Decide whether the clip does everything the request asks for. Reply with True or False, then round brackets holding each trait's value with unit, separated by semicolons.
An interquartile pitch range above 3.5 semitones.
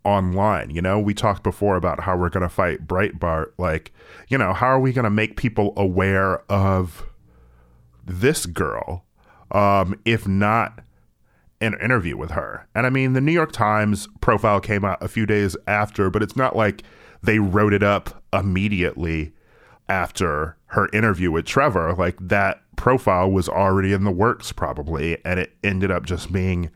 False (2.7 semitones)